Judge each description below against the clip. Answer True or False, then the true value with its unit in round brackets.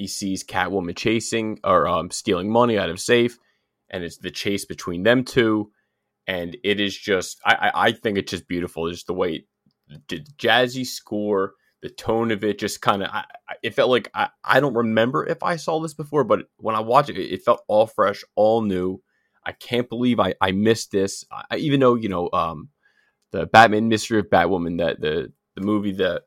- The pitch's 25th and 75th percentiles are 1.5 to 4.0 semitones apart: True (3.7 semitones)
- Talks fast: True (210 wpm)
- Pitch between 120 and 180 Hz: False (105 Hz)